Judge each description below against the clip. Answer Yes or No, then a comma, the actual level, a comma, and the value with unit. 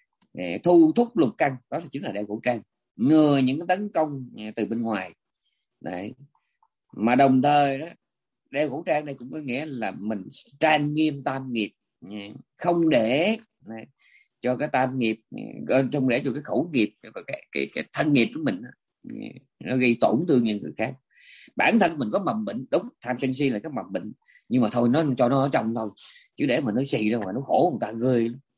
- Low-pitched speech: Yes, low, 130 Hz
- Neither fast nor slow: Yes, average, 215 wpm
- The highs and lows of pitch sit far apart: No, average, 4.5 semitones